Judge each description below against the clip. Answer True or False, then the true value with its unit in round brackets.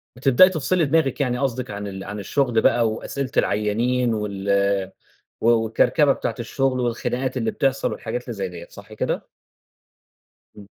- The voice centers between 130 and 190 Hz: False (120 Hz)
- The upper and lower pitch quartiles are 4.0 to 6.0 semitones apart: True (4.6 semitones)